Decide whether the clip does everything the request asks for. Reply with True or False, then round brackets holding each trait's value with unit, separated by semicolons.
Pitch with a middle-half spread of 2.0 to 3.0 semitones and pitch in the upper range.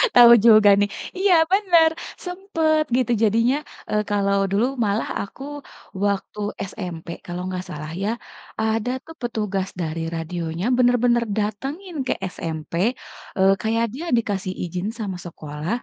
False (5.2 semitones; 210 Hz)